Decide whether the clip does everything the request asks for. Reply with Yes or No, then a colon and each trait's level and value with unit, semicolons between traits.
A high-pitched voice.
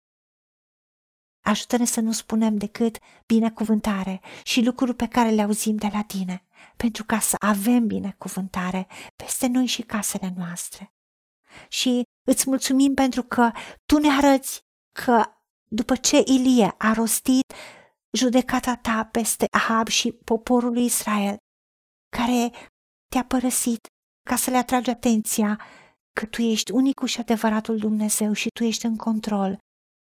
Yes: high, 230 Hz